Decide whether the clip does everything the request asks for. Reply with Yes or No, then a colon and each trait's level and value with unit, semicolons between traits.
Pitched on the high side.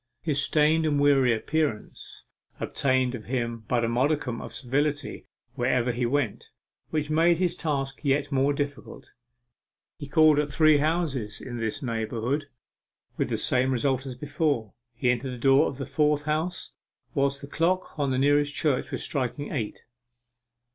No: medium, 140 Hz